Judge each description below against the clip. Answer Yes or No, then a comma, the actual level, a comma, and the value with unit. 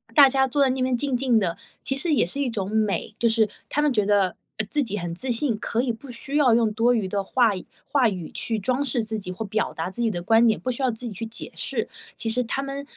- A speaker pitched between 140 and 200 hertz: No, high, 230 Hz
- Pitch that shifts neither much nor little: Yes, average, 3.7 semitones